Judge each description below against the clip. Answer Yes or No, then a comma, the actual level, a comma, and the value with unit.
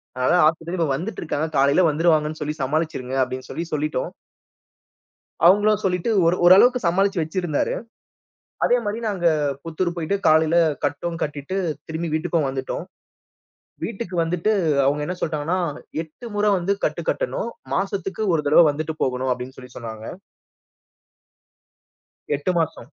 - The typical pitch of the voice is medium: Yes, medium, 165 Hz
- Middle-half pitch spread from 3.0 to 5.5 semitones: Yes, average, 4.0 semitones